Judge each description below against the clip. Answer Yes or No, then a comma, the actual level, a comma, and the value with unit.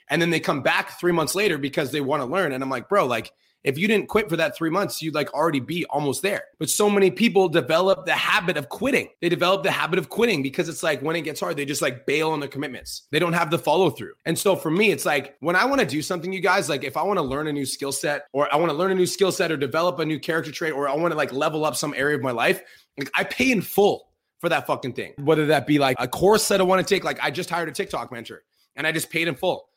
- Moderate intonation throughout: Yes, average, 3.9 semitones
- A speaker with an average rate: No, fast, 305 wpm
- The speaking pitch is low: No, medium, 165 Hz